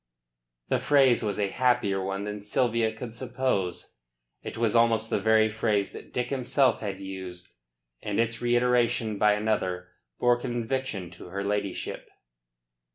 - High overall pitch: No, low, 110 Hz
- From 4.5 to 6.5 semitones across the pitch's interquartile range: No, average, 3.4 semitones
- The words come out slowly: No, average, 145 wpm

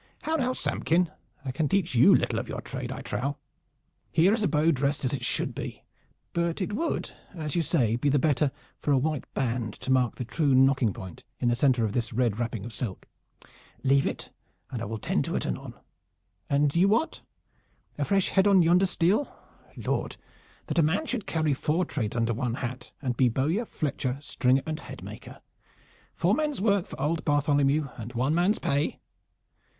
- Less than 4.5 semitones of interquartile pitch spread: No, wide, 5.4 semitones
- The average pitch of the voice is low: No, medium, 145 Hz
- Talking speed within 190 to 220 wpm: Yes, average, 195 wpm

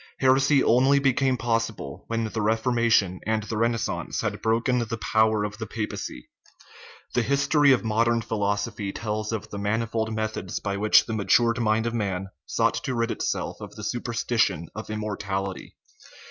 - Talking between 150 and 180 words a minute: Yes, average, 160 wpm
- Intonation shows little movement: Yes, narrow, 1.9 semitones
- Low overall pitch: Yes, low, 110 Hz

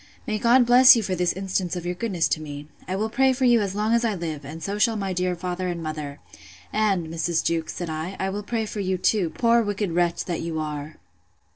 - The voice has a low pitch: No, medium, 185 Hz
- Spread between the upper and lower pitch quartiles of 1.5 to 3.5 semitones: No, average, 4.5 semitones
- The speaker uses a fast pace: Yes, fast, 245 wpm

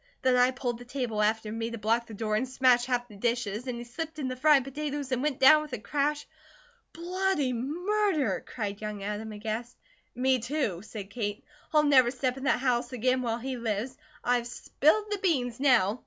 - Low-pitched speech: No, very high, 250 Hz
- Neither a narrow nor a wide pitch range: Yes, average, 3.7 semitones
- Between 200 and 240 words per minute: Yes, fast, 205 wpm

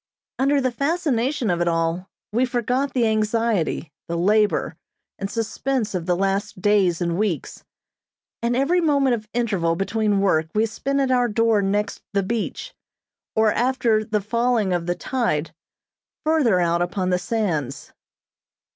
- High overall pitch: Yes, high, 215 Hz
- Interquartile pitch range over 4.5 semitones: Yes, average, 5.0 semitones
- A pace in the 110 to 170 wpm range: Yes, average, 150 wpm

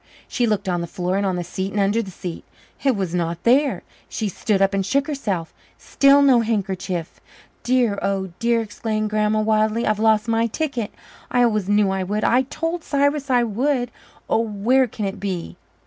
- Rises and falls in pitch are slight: No, average, 3.9 semitones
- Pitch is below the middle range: No, high, 215 Hz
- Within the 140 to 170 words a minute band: No, average, 195 wpm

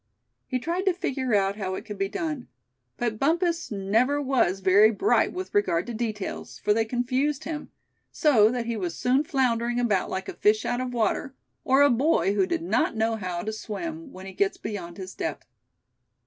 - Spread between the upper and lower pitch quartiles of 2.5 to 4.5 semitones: No, average, 5.3 semitones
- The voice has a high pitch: Yes, high, 235 Hz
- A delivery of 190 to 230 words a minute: Yes, average, 195 wpm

